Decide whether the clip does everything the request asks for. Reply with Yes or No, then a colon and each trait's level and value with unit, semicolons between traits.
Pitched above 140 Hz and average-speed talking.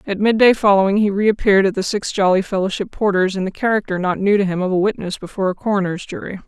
No: high, 195 Hz; fast, 240 wpm